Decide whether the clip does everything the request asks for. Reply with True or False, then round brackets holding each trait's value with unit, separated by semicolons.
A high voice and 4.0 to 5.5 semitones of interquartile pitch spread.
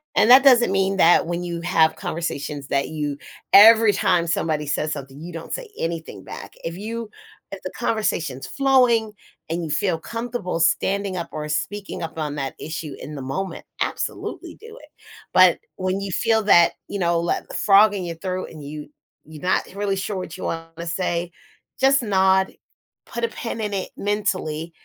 False (180 Hz; 4.4 semitones)